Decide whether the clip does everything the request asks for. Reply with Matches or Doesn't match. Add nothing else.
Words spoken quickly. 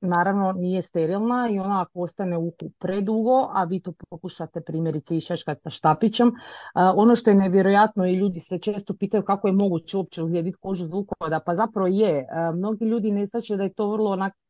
Doesn't match